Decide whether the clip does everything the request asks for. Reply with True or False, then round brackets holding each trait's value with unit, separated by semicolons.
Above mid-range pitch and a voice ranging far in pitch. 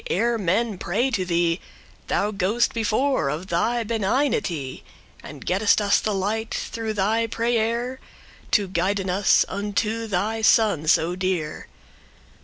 False (205 Hz; 3.6 semitones)